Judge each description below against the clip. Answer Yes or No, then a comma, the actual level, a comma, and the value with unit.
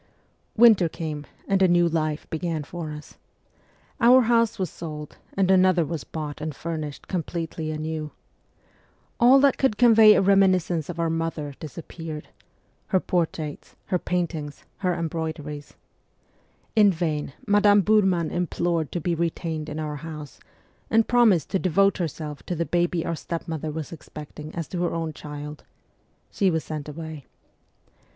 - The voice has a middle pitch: Yes, medium, 165 Hz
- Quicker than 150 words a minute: No, average, 145 wpm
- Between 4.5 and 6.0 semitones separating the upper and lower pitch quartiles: No, average, 3.2 semitones